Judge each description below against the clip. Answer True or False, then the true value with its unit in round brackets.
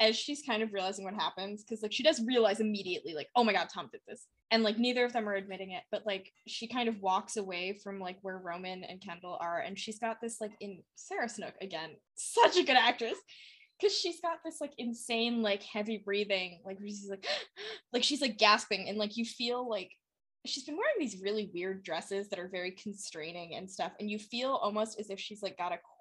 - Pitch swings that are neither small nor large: True (3.7 semitones)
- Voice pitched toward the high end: True (210 Hz)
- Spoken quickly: True (230 wpm)